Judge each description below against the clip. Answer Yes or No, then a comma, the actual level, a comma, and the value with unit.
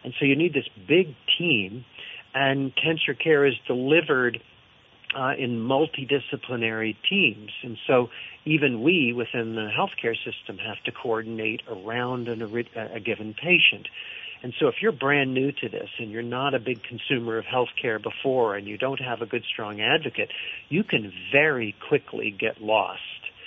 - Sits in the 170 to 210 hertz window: No, low, 125 Hz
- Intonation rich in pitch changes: No, average, 3.8 semitones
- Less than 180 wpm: Yes, average, 165 wpm